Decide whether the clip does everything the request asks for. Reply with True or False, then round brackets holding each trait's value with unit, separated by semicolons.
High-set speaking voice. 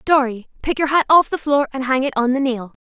True (270 Hz)